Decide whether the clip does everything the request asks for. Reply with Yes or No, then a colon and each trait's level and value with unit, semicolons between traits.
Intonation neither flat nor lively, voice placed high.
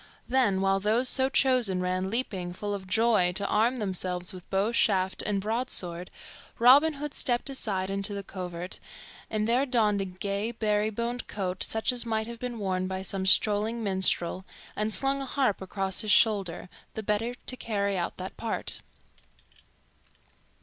Yes: average, 3.7 semitones; high, 210 Hz